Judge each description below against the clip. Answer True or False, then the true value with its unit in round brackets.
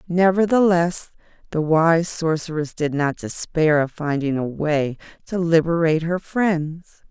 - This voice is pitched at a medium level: True (160 Hz)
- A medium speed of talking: False (125 wpm)